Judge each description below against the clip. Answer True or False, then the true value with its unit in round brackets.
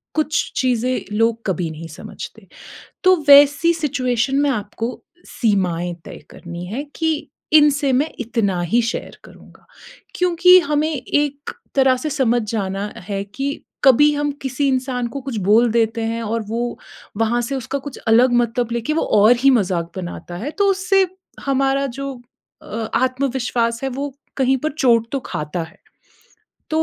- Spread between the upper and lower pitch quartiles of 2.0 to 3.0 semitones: False (3.9 semitones)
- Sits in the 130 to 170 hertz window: False (250 Hz)